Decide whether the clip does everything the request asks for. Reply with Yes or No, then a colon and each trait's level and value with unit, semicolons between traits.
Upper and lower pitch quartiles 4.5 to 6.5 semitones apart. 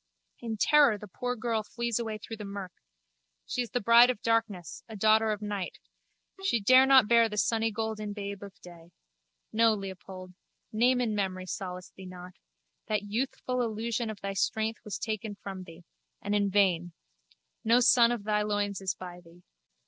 No: average, 2.8 semitones